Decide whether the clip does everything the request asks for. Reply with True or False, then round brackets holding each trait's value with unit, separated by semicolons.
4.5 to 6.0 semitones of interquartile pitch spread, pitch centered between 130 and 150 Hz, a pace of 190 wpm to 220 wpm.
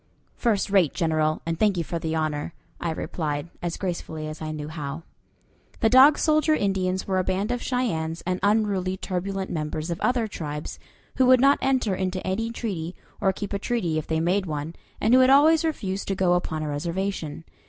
False (5.2 semitones; 185 Hz; 195 wpm)